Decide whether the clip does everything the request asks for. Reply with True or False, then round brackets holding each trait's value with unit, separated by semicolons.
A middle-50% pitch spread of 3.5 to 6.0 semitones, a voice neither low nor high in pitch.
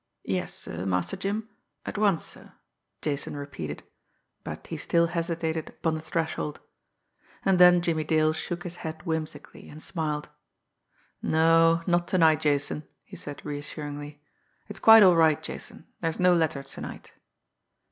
False (2.6 semitones; 160 Hz)